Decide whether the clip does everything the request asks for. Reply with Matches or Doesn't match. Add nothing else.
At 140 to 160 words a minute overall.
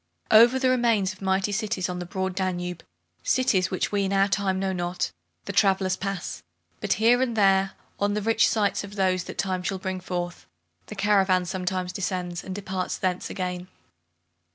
Doesn't match